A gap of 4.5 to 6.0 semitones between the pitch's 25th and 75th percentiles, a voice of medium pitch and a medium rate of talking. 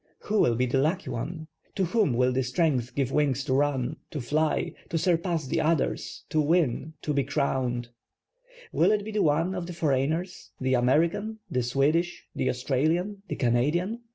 Yes: average, 4.8 semitones; medium, 150 Hz; average, 175 wpm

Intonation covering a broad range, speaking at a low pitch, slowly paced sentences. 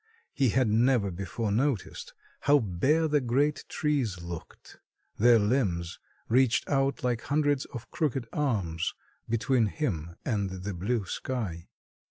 Yes: wide, 5.7 semitones; low, 120 Hz; slow, 130 wpm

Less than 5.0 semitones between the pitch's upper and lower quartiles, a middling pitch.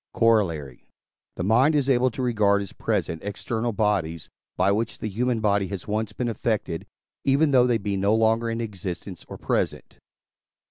No: average, 3.1 semitones; low, 110 Hz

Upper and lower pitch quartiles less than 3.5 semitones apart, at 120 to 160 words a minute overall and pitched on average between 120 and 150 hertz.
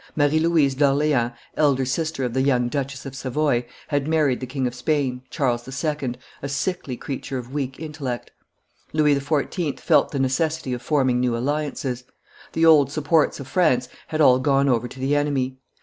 No: average, 2.8 semitones; average, 175 wpm; medium, 140 Hz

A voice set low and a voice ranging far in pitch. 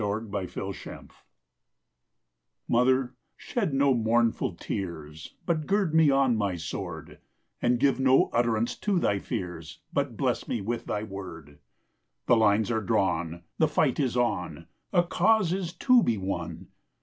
Yes: low, 115 Hz; wide, 6.3 semitones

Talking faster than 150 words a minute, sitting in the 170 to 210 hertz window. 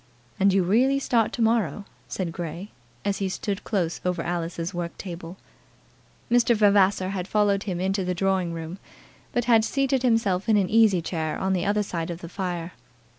Yes: average, 180 wpm; high, 190 Hz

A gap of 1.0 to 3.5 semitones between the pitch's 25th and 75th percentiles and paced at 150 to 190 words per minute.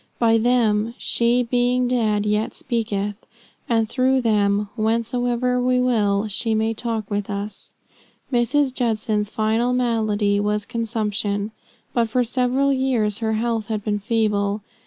No: average, 2.7 semitones; slow, 135 wpm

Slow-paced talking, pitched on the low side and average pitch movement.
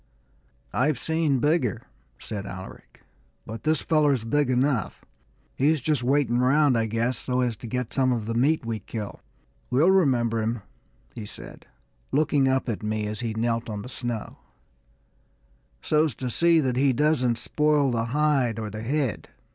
No: average, 165 wpm; low, 125 Hz; average, 4.3 semitones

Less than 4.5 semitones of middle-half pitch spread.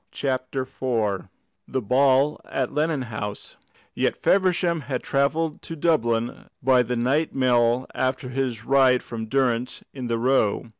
Yes: narrow, 2.6 semitones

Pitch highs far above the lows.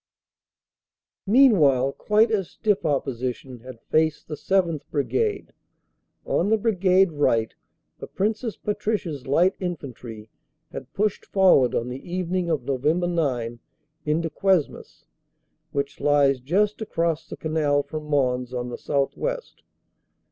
Yes: wide, 6.1 semitones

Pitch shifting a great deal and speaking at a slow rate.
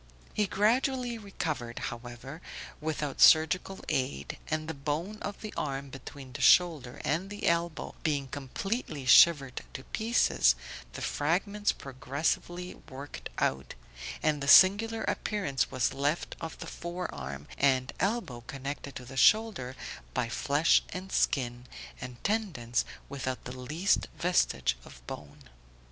Yes: wide, 6.1 semitones; slow, 130 wpm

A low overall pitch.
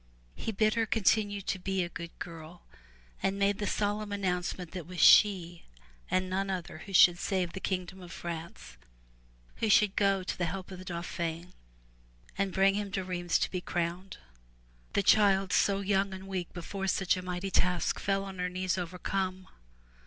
No: medium, 185 Hz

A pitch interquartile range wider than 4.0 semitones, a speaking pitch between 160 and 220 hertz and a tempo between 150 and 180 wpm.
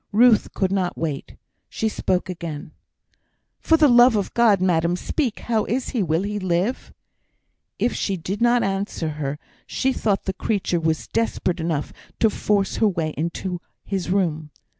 Yes: average, 4.6 semitones; high, 190 Hz; average, 160 wpm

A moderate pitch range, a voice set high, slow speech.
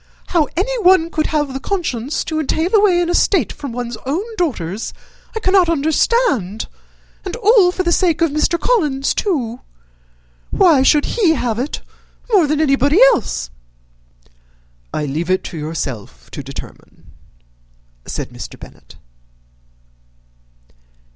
No: wide, 7.0 semitones; very high, 310 Hz; slow, 130 wpm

